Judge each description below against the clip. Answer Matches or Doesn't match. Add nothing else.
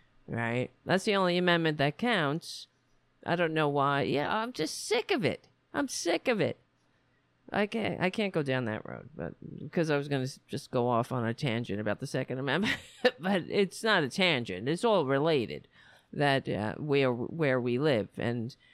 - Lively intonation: Matches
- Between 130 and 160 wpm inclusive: Doesn't match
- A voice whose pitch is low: Doesn't match